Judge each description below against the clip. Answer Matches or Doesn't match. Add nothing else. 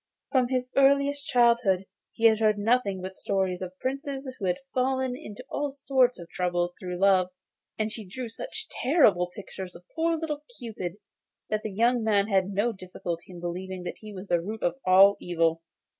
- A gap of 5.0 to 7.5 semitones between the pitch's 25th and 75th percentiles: Matches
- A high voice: Matches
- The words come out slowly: Doesn't match